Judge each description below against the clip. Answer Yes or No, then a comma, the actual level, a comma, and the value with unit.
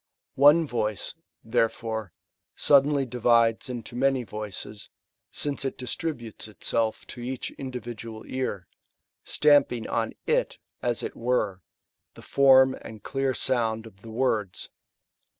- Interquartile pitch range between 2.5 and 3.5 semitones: Yes, average, 3.0 semitones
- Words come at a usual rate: No, slow, 115 wpm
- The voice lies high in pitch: No, low, 120 Hz